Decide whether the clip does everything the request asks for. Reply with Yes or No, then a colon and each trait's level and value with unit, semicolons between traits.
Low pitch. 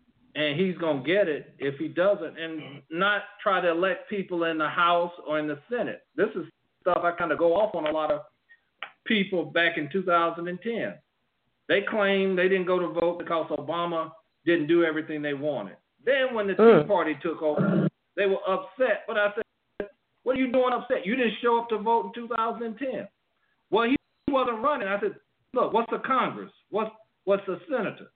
No: high, 190 Hz